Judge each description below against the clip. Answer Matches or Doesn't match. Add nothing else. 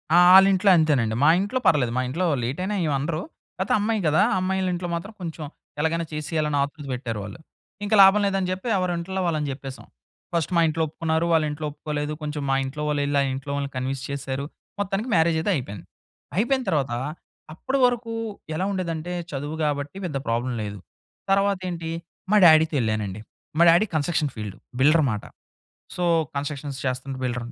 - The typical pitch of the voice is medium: Matches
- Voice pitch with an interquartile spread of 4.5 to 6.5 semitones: Matches